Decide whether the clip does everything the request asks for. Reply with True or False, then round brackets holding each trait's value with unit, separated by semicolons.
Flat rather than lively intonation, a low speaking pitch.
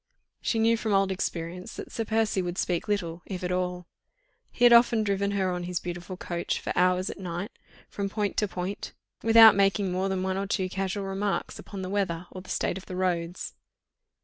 False (2.0 semitones; 190 Hz)